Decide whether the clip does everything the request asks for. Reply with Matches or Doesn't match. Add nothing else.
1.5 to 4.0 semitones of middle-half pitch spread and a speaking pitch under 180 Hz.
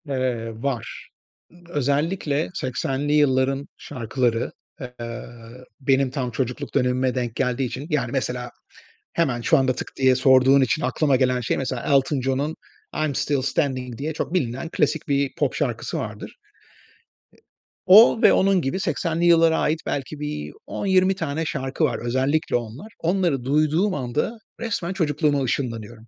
Matches